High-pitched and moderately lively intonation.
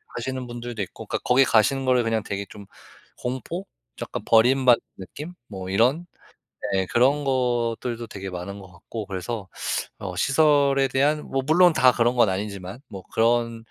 No: low, 120 Hz; average, 4.9 semitones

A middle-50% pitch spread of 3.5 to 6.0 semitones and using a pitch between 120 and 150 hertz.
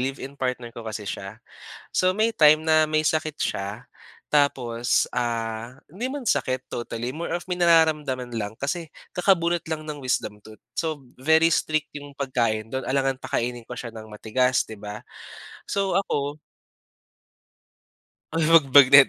Yes: average, 5.0 semitones; low, 135 Hz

